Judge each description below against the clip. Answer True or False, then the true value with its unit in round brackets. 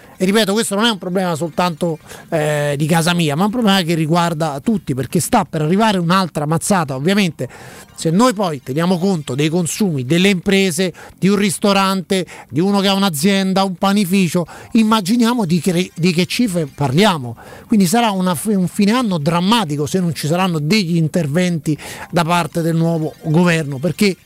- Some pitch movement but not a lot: True (3.3 semitones)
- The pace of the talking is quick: True (175 wpm)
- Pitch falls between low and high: True (180 Hz)